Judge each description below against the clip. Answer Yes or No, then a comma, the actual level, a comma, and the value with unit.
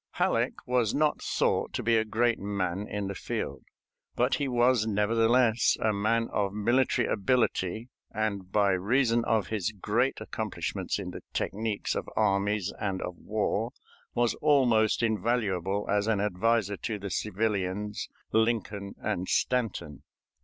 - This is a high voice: No, low, 110 Hz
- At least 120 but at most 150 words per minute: Yes, average, 140 wpm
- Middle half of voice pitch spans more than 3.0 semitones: No, average, 2.7 semitones